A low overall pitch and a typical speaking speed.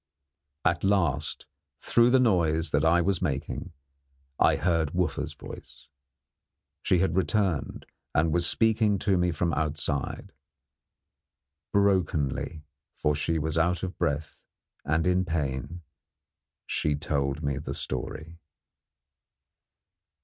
No: very low, 80 Hz; slow, 115 wpm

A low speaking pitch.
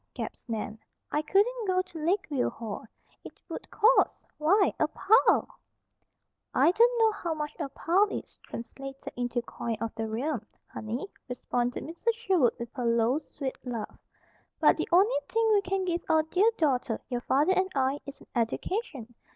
No: very high, 300 Hz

